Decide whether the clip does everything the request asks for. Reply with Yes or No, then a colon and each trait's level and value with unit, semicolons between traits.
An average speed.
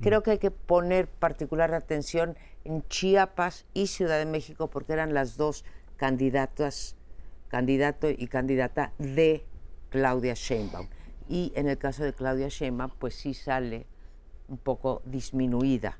Yes: average, 140 wpm